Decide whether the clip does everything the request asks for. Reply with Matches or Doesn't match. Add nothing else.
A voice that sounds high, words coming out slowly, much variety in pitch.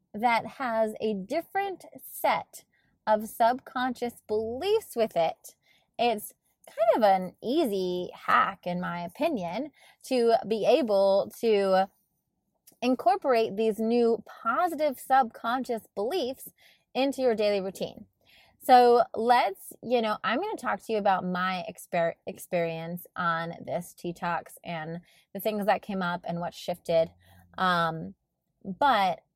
Matches